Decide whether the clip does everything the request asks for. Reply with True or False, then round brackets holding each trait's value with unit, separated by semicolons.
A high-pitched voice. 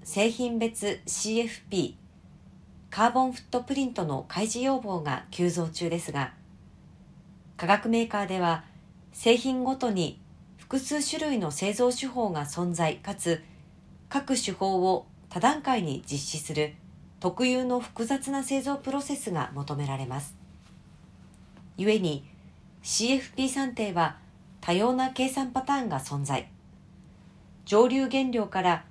True (210 Hz)